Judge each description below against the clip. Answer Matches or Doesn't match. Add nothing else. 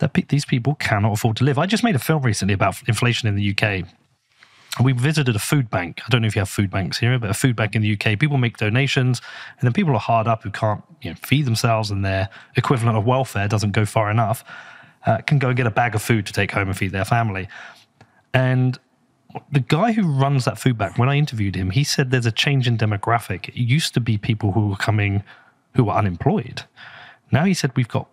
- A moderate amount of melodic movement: Matches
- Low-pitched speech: Matches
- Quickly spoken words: Matches